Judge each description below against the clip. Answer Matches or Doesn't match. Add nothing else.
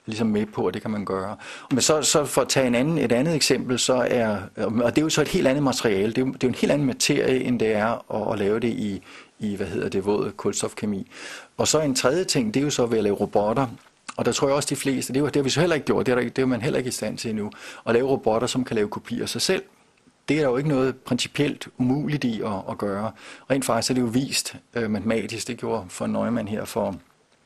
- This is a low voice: Matches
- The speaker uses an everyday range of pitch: Matches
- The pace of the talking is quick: Matches